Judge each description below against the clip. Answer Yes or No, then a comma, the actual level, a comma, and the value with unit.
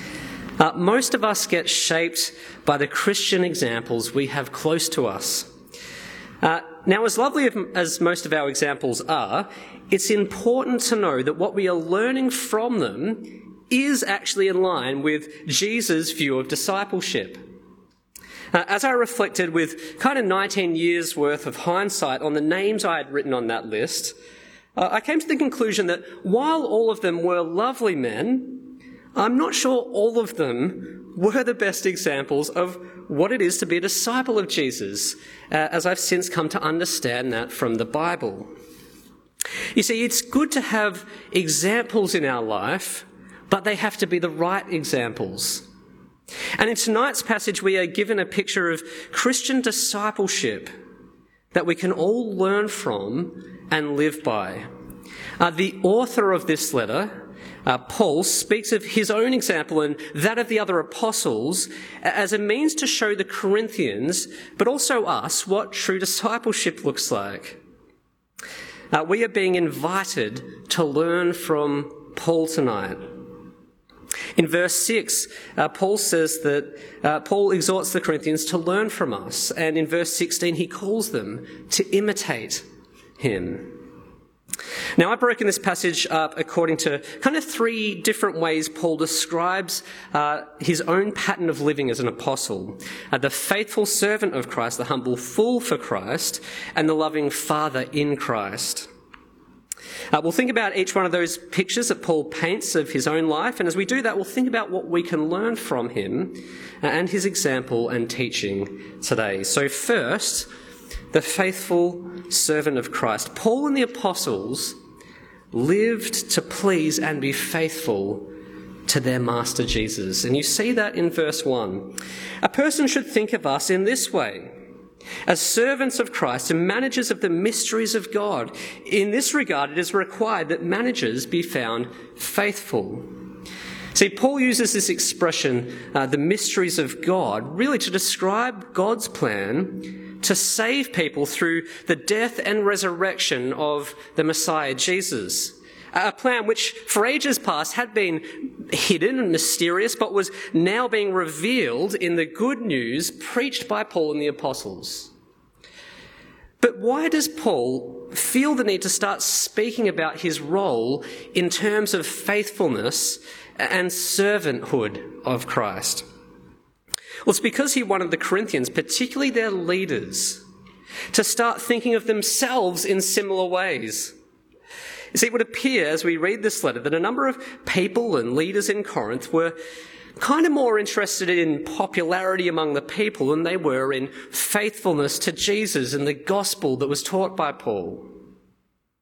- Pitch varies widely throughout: Yes, wide, 5.9 semitones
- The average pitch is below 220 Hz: Yes, medium, 185 Hz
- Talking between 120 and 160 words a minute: Yes, average, 155 wpm